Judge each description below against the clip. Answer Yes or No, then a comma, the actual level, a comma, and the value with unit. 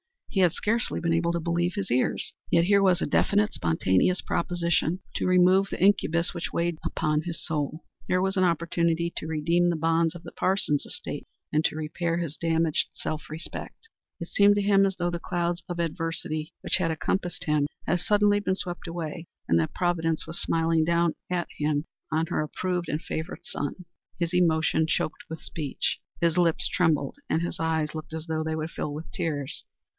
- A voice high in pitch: No, medium, 170 Hz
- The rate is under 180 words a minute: No, average, 190 wpm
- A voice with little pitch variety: Yes, narrow, 2.0 semitones